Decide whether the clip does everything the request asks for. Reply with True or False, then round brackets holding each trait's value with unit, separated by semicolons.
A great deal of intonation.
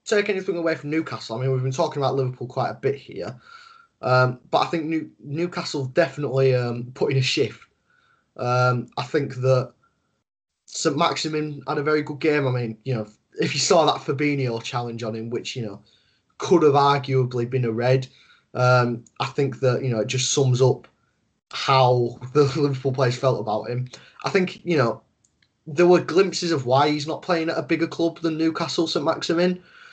False (4.5 semitones)